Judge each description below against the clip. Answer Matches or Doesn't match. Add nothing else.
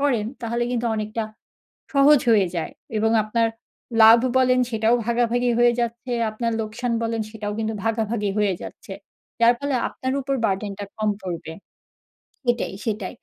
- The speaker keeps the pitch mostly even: Matches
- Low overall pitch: Doesn't match